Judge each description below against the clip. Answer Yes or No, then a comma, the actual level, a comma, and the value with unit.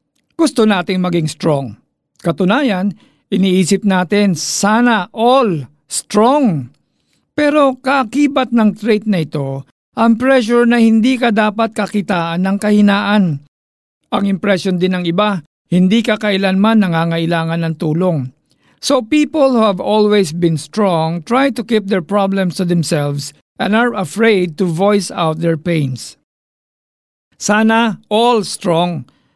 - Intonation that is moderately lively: Yes, average, 5.0 semitones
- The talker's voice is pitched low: No, high, 200 Hz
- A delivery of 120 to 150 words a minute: Yes, average, 125 wpm